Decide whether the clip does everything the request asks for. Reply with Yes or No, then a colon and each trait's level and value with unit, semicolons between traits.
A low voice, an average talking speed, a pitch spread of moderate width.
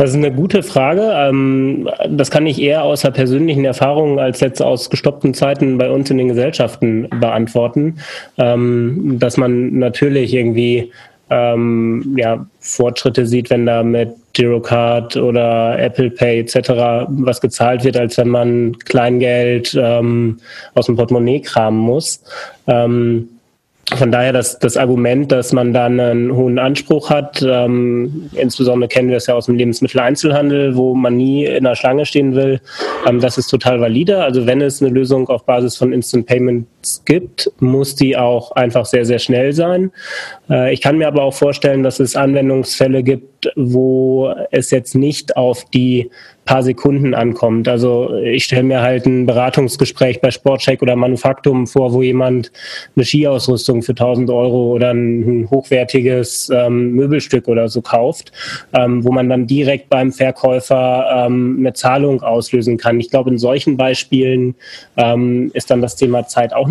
No: low, 125 Hz; average, 160 wpm; narrow, 1.8 semitones